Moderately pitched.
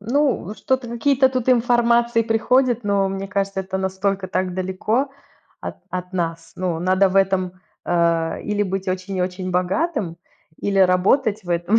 No: high, 195 Hz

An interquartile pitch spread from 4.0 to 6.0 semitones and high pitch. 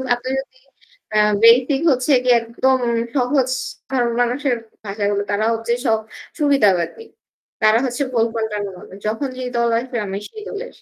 No: average, 3.1 semitones; high, 240 Hz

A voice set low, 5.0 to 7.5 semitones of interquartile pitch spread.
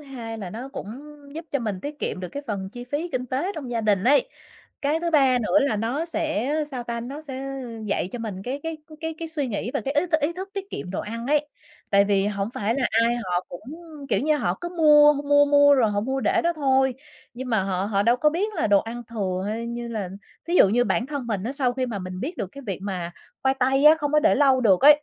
No: very high, 255 Hz; wide, 5.5 semitones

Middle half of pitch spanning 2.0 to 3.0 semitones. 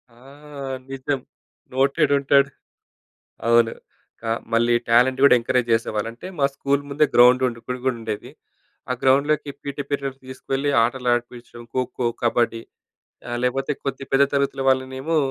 Yes: narrow, 2.5 semitones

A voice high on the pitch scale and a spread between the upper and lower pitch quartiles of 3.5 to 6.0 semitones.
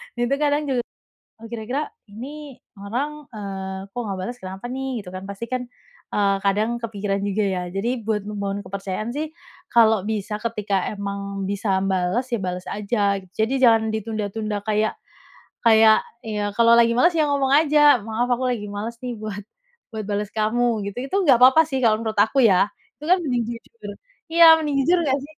Yes: high, 220 Hz; average, 4.0 semitones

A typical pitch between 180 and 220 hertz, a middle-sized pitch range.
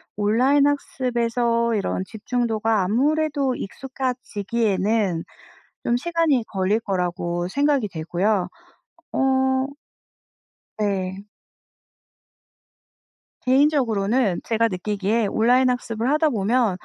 No: high, 230 Hz; average, 4.7 semitones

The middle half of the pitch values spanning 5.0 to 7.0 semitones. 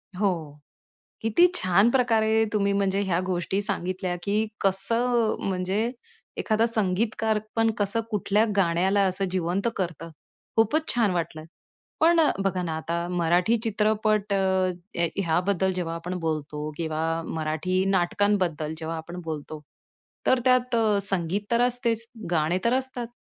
No: average, 4.3 semitones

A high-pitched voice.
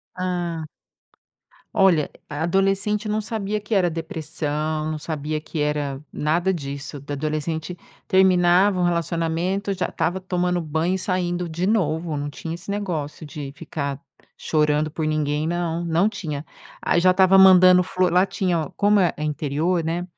No: medium, 170 Hz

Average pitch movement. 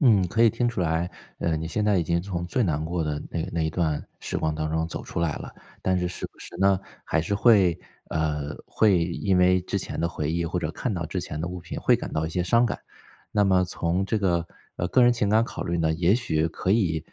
Yes: average, 3.4 semitones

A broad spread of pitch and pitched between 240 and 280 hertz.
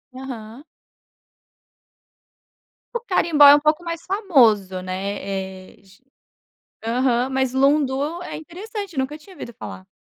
Yes: wide, 7.2 semitones; very high, 265 Hz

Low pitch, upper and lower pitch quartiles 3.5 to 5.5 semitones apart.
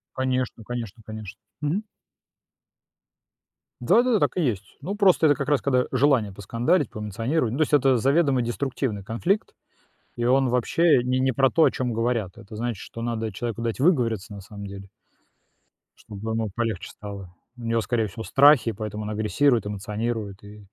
Yes: low, 115 Hz; average, 4.1 semitones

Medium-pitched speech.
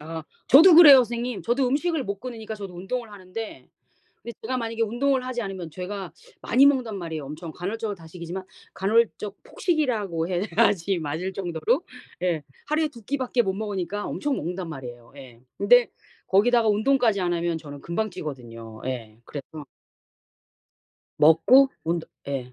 No: high, 200 Hz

